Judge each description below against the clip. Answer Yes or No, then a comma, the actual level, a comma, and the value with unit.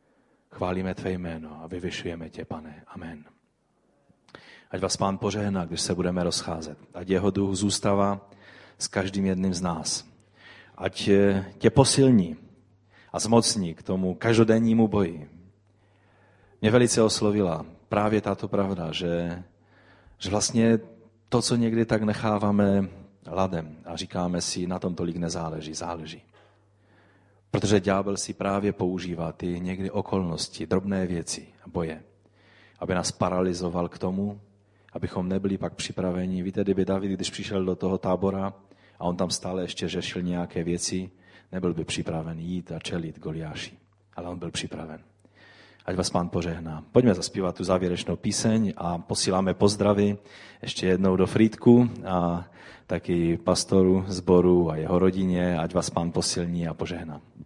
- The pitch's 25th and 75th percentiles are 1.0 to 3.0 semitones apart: Yes, average, 2.7 semitones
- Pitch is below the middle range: Yes, very low, 95 Hz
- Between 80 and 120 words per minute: No, average, 140 wpm